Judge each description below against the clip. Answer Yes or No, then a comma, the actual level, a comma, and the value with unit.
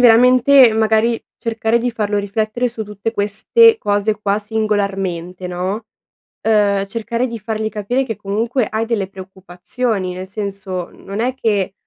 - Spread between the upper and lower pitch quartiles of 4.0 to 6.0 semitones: No, average, 2.7 semitones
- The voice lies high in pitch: Yes, high, 215 Hz